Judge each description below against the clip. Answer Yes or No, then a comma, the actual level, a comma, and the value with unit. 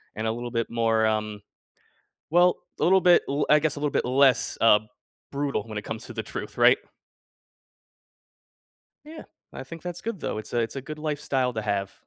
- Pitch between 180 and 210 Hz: No, low, 130 Hz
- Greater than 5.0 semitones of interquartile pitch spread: Yes, wide, 5.5 semitones